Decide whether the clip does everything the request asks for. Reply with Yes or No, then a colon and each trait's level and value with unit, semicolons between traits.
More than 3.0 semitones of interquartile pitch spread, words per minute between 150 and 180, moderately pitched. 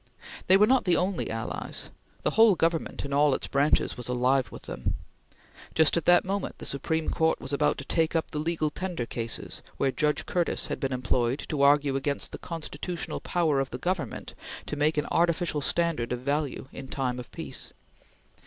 No: average, 3.9 semitones; average, 190 wpm; medium, 150 Hz